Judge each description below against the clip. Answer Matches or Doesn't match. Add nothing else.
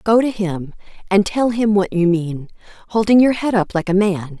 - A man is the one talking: Doesn't match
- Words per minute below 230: Matches